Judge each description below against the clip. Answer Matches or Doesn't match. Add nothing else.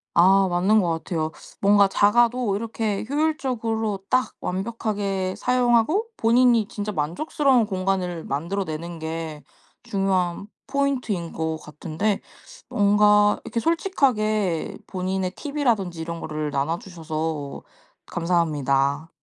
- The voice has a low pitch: Doesn't match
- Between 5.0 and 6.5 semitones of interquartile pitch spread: Matches